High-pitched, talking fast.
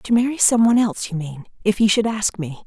Yes: high, 210 Hz; fast, 250 wpm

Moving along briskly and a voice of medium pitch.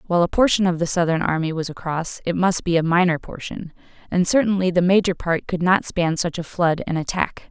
Yes: fast, 225 wpm; medium, 175 Hz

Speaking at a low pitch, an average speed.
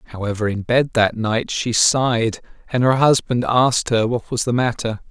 Yes: low, 120 Hz; average, 190 wpm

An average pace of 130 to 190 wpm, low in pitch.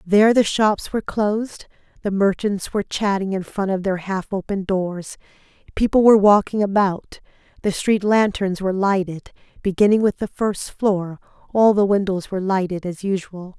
No: average, 165 wpm; high, 195 Hz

